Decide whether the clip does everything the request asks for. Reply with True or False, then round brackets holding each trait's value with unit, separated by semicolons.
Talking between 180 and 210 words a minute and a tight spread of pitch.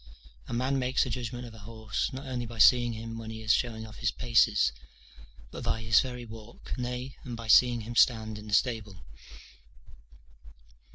True (185 wpm; 1.9 semitones)